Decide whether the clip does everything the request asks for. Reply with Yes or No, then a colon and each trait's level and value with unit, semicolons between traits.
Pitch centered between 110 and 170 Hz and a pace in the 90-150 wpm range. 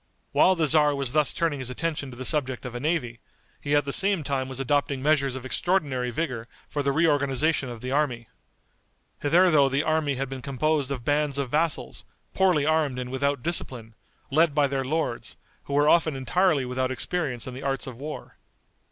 No: medium, 140 Hz; average, 195 wpm